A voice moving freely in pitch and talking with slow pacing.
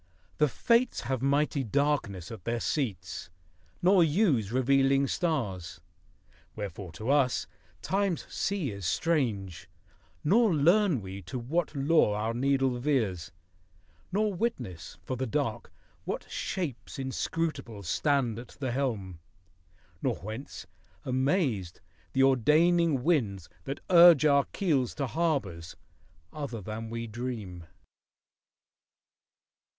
Yes: wide, 6.2 semitones; slow, 115 wpm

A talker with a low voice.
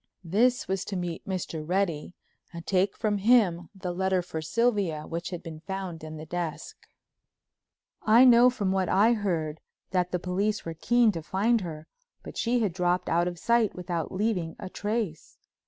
No: medium, 185 Hz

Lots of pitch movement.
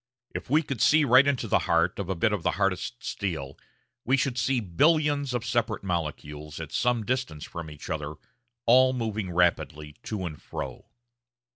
Yes: wide, 7.4 semitones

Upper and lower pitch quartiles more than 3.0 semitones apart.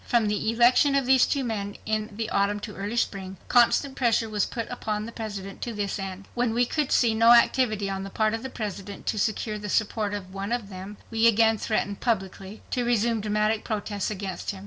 No: narrow, 2.5 semitones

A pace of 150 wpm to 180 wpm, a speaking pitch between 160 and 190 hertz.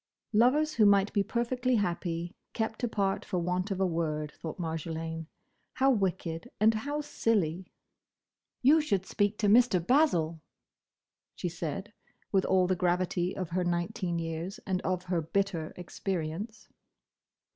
No: average, 140 wpm; medium, 185 Hz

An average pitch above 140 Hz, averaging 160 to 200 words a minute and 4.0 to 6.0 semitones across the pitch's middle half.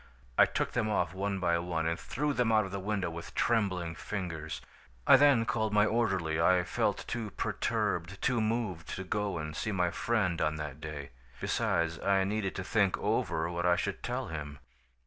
No: very low, 95 Hz; average, 190 wpm; average, 4.5 semitones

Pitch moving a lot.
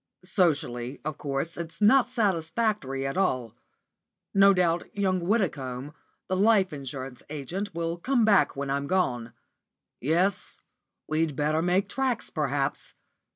Yes: wide, 5.9 semitones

